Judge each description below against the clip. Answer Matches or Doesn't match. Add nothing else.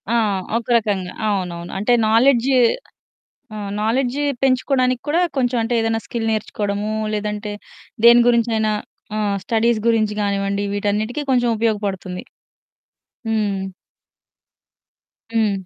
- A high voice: Matches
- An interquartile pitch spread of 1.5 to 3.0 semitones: Matches